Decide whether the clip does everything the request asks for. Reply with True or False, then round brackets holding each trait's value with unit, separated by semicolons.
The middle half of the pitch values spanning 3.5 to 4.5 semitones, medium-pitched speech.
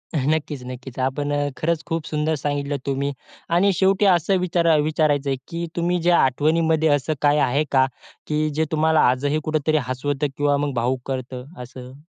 False (2.8 semitones; 150 Hz)